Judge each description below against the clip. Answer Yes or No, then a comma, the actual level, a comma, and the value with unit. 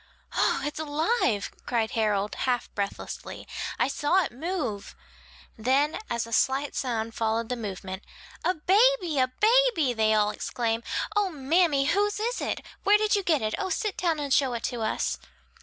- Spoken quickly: No, average, 170 wpm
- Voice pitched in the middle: No, very high, 275 Hz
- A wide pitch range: Yes, wide, 8.2 semitones